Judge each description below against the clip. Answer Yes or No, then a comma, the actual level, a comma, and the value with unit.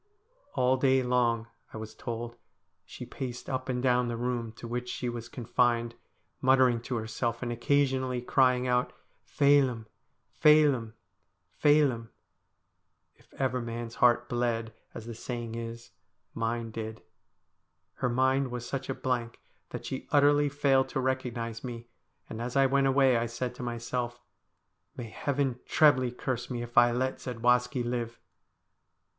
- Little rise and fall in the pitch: Yes, narrow, 2.0 semitones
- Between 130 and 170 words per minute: Yes, average, 150 wpm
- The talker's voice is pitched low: Yes, low, 125 Hz